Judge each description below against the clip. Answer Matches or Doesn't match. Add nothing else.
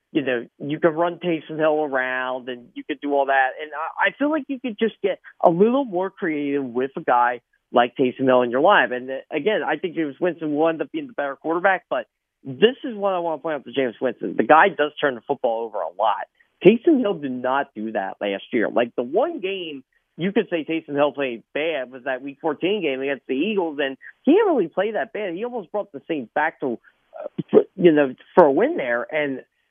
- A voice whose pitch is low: Doesn't match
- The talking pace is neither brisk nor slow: Doesn't match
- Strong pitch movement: Matches